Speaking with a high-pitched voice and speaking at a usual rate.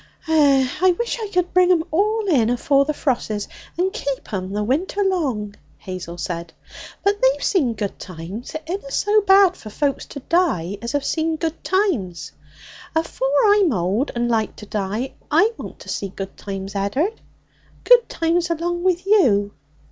Yes: very high, 285 Hz; average, 170 wpm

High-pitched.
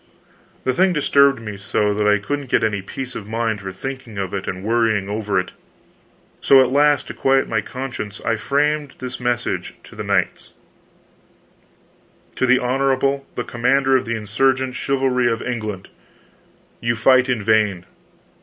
No: low, 120 Hz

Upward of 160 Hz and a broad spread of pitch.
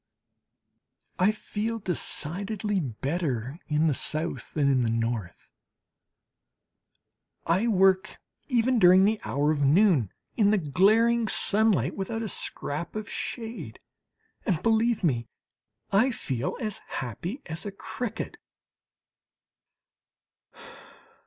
Yes: high, 190 Hz; wide, 7.1 semitones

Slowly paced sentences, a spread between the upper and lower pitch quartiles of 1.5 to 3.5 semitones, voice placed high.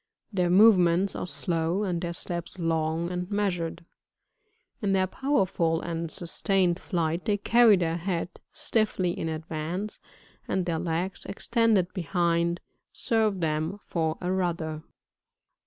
No: slow, 125 wpm; average, 2.7 semitones; medium, 175 Hz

